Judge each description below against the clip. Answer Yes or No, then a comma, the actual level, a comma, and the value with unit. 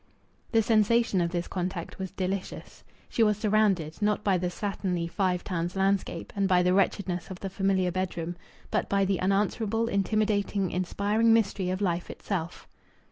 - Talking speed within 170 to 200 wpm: No, average, 160 wpm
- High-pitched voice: Yes, high, 195 Hz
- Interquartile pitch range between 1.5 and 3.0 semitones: Yes, narrow, 2.4 semitones